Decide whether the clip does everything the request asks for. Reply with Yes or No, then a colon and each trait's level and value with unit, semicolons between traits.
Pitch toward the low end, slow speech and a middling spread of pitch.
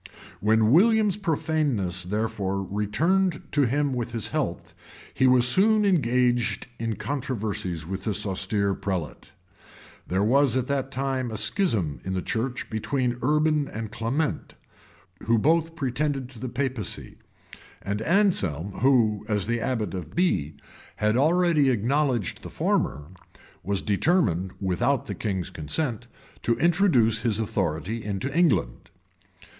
No: low, 120 Hz; slow, 130 wpm; wide, 6.0 semitones